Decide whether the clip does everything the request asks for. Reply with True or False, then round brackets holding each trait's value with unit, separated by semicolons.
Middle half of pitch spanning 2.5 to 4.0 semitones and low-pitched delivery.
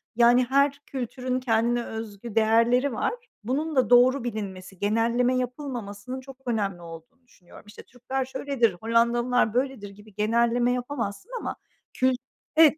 False (2.8 semitones; 240 Hz)